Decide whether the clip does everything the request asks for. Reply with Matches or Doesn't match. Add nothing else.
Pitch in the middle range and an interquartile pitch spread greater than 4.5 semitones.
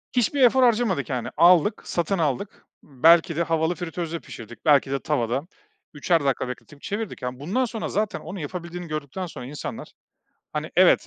Matches